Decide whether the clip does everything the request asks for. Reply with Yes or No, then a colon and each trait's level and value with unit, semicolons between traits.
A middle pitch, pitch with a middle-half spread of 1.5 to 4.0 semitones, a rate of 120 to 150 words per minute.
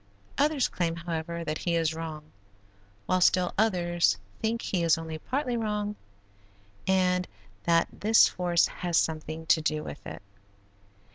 Yes: medium, 175 Hz; average, 2.9 semitones; average, 140 wpm